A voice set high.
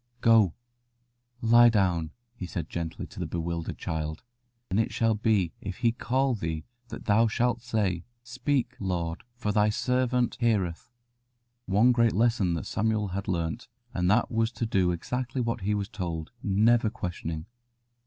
No: low, 105 Hz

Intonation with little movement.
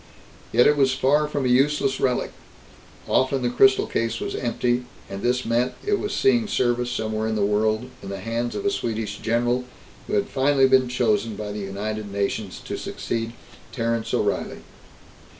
No: average, 3.3 semitones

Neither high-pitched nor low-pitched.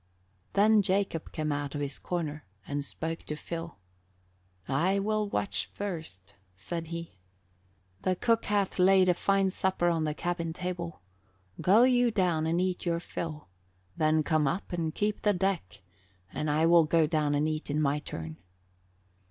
Yes: medium, 170 Hz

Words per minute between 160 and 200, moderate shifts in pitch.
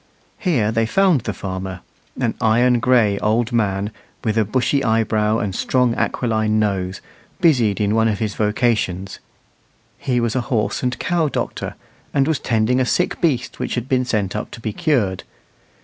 Yes: average, 170 wpm; average, 3.2 semitones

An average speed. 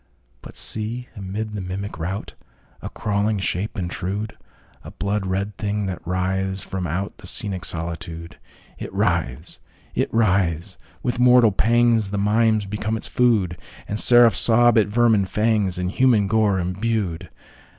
No: slow, 115 wpm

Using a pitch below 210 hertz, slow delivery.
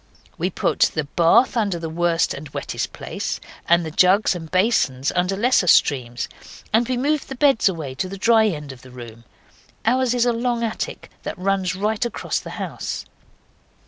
No: medium, 185 Hz; average, 180 wpm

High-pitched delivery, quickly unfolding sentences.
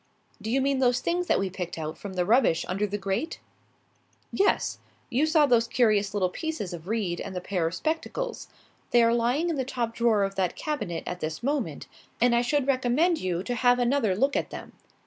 Yes: high, 235 Hz; fast, 210 wpm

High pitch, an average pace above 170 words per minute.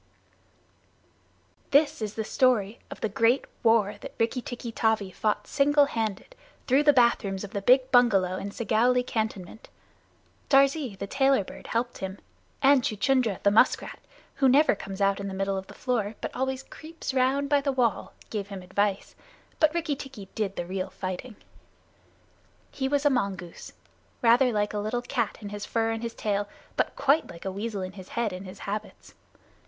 Yes: high, 225 Hz; average, 180 wpm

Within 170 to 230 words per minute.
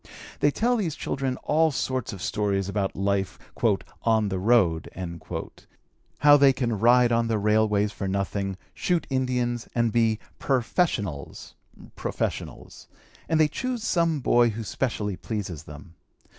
No: slow, 135 wpm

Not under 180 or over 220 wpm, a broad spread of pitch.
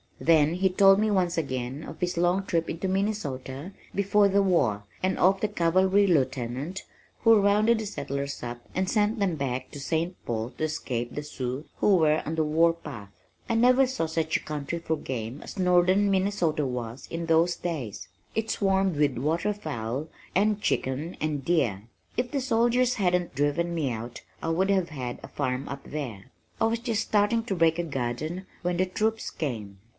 Yes: average, 185 wpm; wide, 5.9 semitones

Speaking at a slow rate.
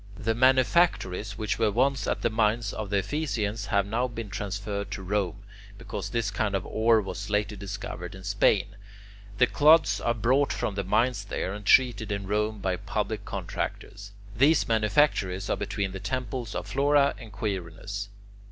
No: average, 170 wpm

